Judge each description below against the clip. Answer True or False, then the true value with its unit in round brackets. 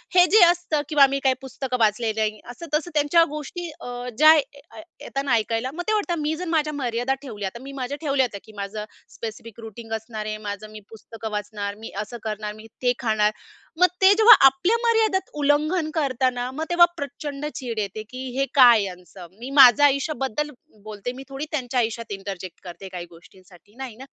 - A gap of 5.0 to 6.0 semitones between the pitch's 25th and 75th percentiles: True (5.5 semitones)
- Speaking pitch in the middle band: False (255 Hz)